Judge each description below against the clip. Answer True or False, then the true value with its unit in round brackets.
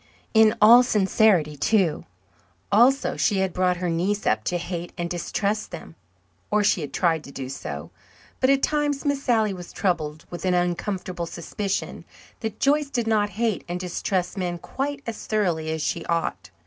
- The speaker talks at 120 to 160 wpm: False (175 wpm)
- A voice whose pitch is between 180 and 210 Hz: True (190 Hz)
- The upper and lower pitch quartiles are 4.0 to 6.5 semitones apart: True (4.4 semitones)